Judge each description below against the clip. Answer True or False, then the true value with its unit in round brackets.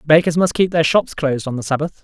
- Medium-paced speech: False (265 wpm)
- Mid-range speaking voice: True (155 Hz)